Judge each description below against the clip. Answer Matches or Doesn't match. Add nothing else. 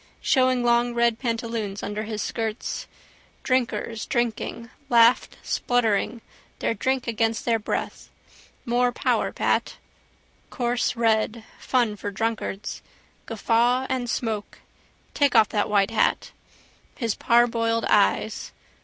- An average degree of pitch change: Doesn't match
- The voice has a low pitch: Doesn't match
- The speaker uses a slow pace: Matches